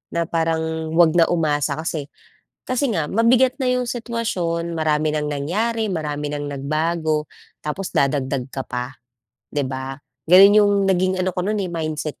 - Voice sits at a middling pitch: Yes, medium, 165 Hz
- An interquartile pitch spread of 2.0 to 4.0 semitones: No, average, 4.6 semitones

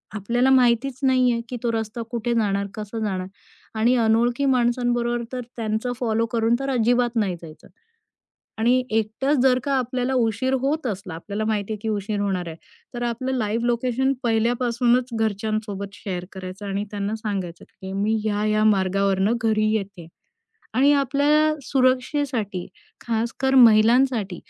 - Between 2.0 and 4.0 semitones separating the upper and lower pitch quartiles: Yes, average, 3.3 semitones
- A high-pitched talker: Yes, high, 225 Hz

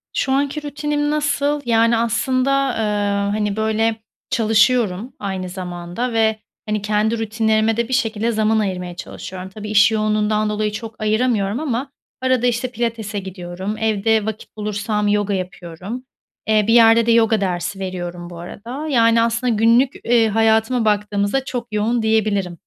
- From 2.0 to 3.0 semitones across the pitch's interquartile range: Yes, narrow, 2.4 semitones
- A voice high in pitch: Yes, high, 220 Hz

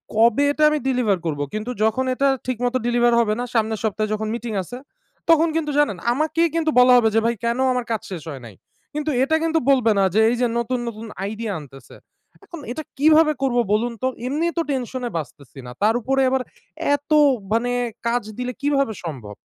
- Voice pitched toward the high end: Yes, high, 240 Hz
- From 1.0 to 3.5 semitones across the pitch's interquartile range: No, average, 4.2 semitones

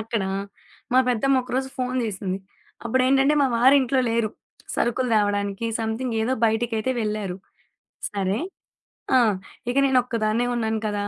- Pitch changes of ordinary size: Yes, average, 3.2 semitones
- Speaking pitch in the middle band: No, high, 230 Hz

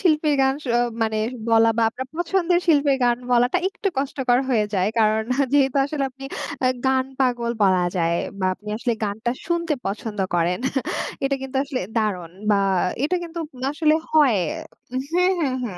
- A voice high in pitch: Yes, very high, 255 Hz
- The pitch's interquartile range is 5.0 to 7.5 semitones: Yes, wide, 5.6 semitones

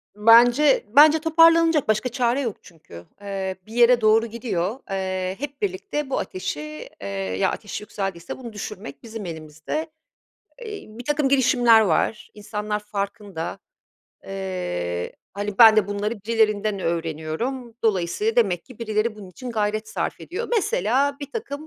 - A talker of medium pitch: No, high, 215 Hz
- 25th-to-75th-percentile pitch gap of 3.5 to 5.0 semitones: No, wide, 5.4 semitones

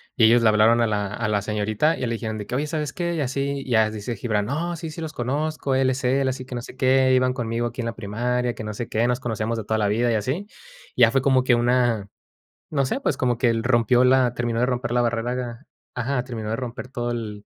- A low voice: Yes, low, 120 Hz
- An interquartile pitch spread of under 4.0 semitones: Yes, narrow, 2.5 semitones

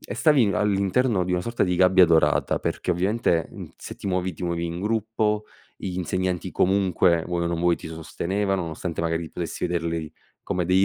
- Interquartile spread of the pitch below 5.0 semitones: Yes, average, 2.7 semitones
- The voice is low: Yes, very low, 90 Hz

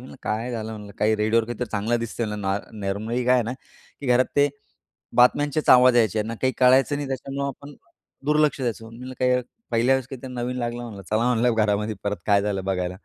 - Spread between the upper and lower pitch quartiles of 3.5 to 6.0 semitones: No, average, 3.0 semitones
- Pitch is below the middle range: Yes, low, 120 Hz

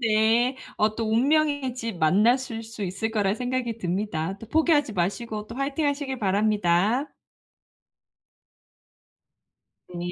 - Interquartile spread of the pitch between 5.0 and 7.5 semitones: No, average, 4.0 semitones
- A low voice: No, high, 225 Hz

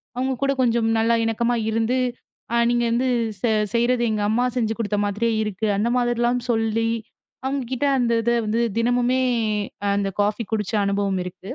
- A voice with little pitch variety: Yes, narrow, 2.1 semitones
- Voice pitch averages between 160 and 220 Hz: No, high, 230 Hz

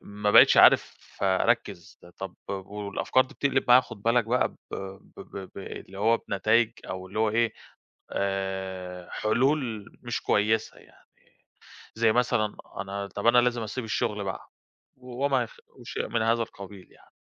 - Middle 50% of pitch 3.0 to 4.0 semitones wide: Yes, average, 3.3 semitones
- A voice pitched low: Yes, low, 105 Hz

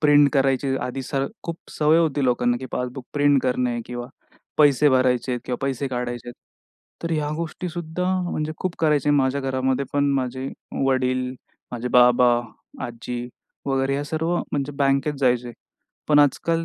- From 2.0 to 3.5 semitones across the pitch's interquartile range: Yes, average, 2.8 semitones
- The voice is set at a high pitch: No, low, 135 Hz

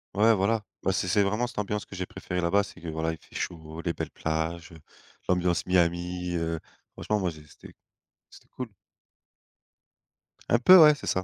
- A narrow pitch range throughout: No, average, 3.8 semitones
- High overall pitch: No, very low, 90 Hz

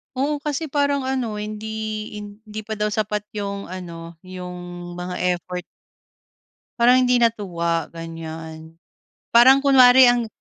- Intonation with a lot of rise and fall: Yes, wide, 5.8 semitones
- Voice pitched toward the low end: No, high, 210 Hz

